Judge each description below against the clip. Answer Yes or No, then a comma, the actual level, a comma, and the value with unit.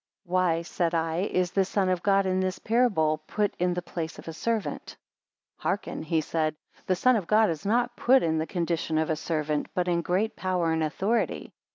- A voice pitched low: No, medium, 180 Hz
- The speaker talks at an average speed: No, fast, 210 wpm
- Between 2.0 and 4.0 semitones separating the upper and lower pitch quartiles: Yes, average, 3.4 semitones